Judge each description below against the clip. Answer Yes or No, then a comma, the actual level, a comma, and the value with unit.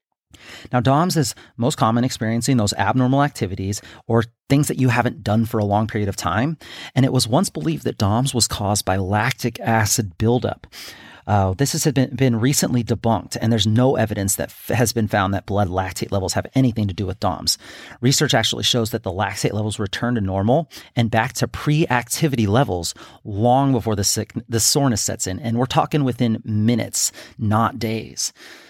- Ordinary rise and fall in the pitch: Yes, average, 3.3 semitones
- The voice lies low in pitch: Yes, low, 115 Hz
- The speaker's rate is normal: Yes, average, 190 wpm